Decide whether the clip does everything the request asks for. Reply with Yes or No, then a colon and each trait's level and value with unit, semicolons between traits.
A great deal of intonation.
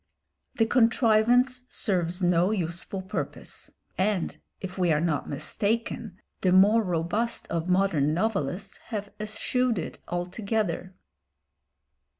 No: average, 4.1 semitones